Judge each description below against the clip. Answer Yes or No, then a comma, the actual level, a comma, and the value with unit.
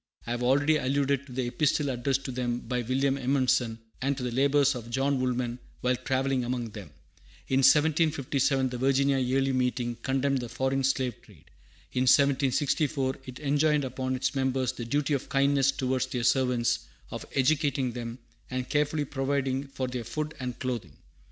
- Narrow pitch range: Yes, narrow, 1.8 semitones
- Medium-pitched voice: No, low, 130 Hz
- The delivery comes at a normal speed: Yes, average, 170 wpm